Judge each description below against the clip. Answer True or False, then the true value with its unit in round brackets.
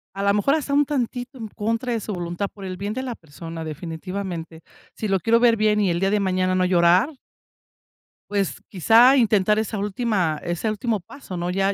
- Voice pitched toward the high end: True (200 Hz)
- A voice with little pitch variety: False (4.0 semitones)